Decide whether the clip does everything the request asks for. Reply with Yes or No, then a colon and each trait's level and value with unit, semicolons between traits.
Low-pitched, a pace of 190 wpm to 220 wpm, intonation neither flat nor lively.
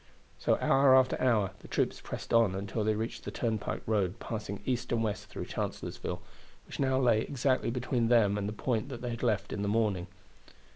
Yes: low, 115 Hz; average, 200 wpm; average, 3.2 semitones